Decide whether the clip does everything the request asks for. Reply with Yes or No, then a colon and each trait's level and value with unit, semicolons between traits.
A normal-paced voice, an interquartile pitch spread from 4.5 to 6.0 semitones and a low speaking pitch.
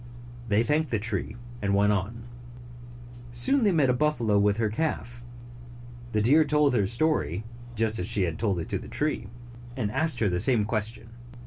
Yes: average, 190 wpm; wide, 5.4 semitones; low, 115 Hz